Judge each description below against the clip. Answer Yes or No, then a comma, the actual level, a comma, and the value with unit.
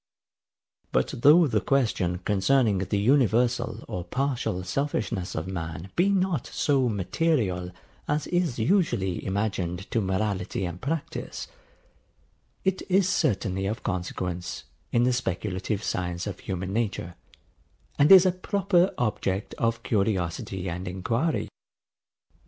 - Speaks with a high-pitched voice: No, low, 105 Hz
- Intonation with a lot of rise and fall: Yes, wide, 7.0 semitones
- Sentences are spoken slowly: Yes, slow, 120 wpm